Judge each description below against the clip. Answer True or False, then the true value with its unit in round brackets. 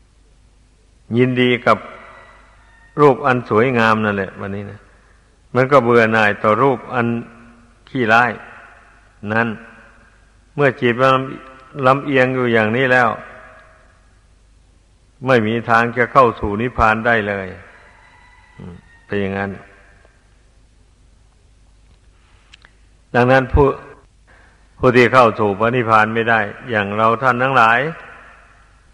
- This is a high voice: False (110 Hz)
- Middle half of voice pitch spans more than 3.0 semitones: True (3.9 semitones)